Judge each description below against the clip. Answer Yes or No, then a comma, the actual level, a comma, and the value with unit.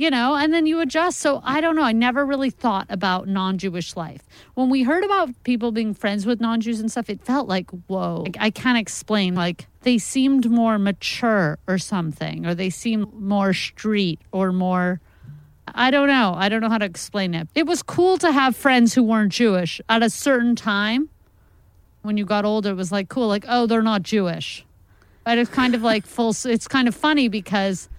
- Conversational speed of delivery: No, fast, 210 wpm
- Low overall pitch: No, high, 215 Hz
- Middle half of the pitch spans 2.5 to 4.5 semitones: No, average, 5.0 semitones